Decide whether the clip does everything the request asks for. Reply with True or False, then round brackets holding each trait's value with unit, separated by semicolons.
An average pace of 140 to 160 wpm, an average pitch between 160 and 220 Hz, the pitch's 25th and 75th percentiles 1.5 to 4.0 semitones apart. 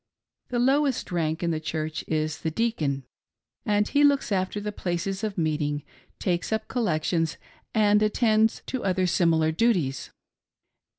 False (150 wpm; 185 Hz; 5.6 semitones)